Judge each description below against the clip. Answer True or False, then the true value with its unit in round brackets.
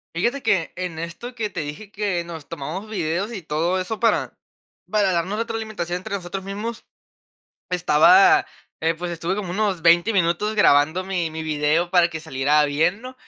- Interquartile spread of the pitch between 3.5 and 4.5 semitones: True (4.2 semitones)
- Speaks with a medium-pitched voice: True (180 Hz)